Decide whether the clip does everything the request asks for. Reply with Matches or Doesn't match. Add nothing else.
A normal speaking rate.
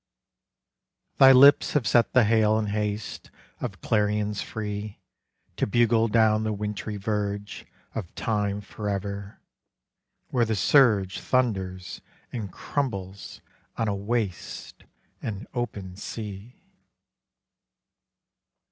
Doesn't match